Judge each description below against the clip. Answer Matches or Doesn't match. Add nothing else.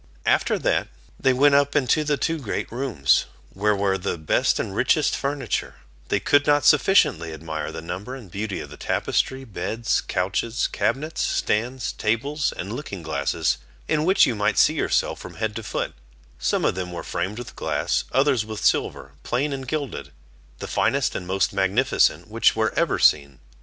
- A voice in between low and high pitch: Doesn't match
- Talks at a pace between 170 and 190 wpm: Matches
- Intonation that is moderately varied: Doesn't match